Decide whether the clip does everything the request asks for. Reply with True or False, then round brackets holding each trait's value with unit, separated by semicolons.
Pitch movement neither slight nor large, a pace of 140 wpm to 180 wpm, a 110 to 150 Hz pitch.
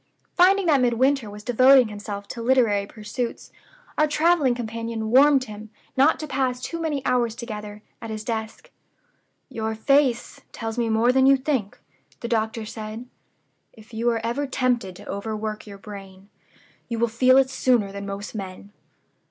False (3.4 semitones; 160 wpm; 230 Hz)